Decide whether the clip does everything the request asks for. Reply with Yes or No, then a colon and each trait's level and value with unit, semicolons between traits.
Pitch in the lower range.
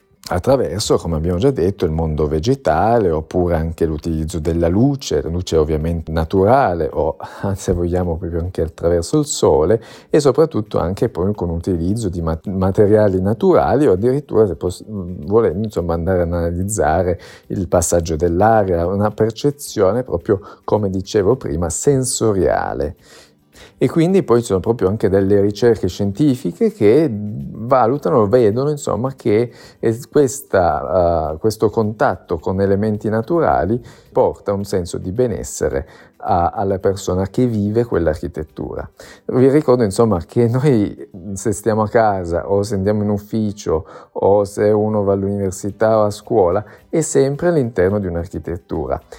Yes: low, 100 Hz